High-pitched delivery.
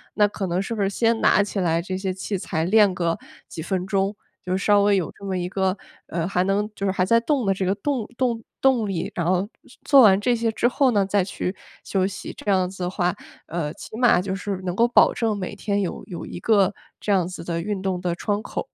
Yes: high, 195 Hz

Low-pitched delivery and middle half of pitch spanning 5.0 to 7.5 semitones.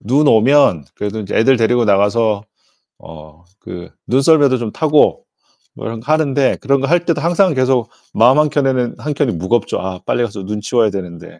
Yes: low, 120 Hz; wide, 5.5 semitones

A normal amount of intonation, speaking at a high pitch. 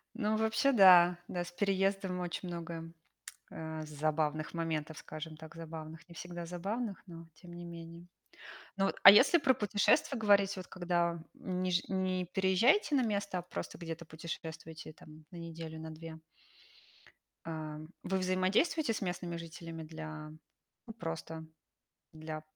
No: average, 3.0 semitones; medium, 175 Hz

